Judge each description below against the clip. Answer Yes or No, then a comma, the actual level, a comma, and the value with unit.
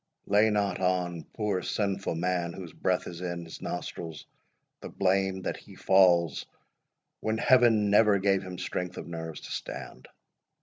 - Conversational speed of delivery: Yes, average, 150 wpm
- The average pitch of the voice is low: Yes, very low, 95 Hz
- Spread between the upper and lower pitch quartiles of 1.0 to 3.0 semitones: Yes, average, 2.7 semitones